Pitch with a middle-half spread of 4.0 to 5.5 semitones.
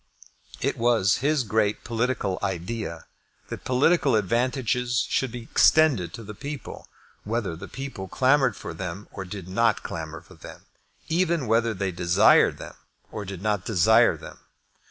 Yes: average, 4.8 semitones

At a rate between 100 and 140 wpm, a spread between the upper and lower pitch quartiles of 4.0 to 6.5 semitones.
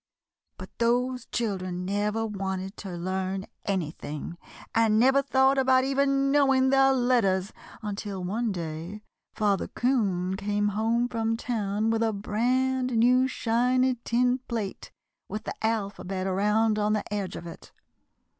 Yes: slow, 135 wpm; average, 4.3 semitones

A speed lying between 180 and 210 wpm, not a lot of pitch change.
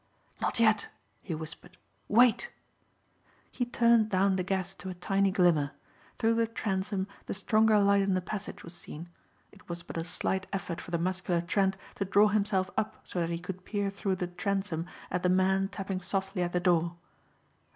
Yes: average, 185 wpm; narrow, 2.3 semitones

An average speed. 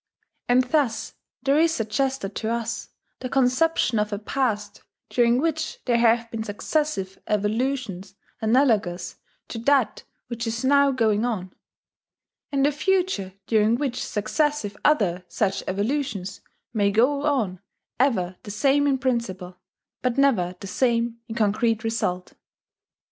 No: slow, 130 wpm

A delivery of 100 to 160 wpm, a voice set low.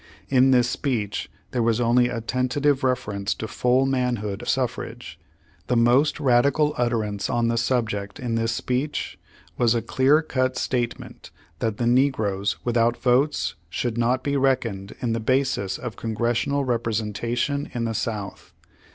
Yes: average, 150 wpm; low, 120 Hz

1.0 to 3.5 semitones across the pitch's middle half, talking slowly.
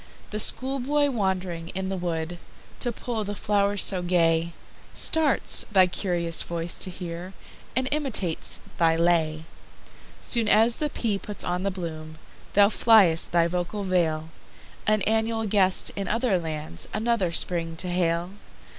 No: average, 4.2 semitones; slow, 120 wpm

